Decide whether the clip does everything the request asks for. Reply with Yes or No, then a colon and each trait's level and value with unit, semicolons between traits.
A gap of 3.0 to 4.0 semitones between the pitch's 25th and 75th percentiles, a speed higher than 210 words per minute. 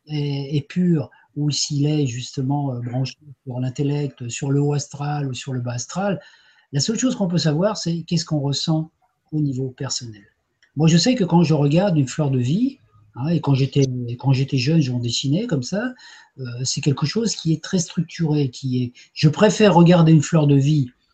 No: average, 3.7 semitones; average, 200 wpm